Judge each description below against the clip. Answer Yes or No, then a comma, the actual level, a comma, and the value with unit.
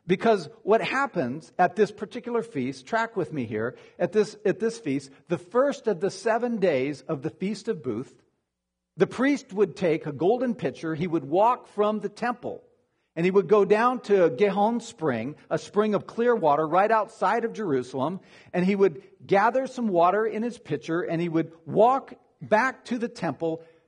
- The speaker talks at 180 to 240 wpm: Yes, average, 185 wpm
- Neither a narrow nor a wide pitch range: No, wide, 5.7 semitones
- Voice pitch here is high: Yes, high, 195 Hz